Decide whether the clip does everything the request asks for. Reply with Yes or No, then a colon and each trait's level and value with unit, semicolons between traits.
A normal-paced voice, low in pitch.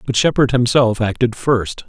Yes: average, 160 wpm; low, 120 Hz